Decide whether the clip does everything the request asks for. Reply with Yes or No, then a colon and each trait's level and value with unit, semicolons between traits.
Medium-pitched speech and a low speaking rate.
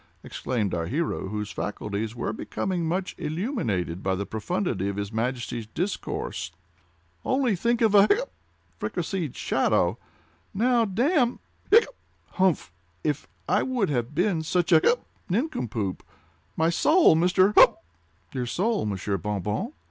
Yes: medium, 160 Hz; slow, 120 wpm